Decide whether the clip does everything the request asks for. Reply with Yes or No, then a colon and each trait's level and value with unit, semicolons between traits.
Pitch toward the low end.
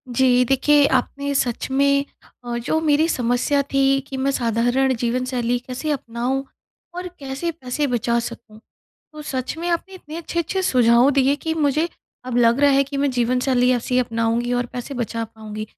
No: very high, 260 Hz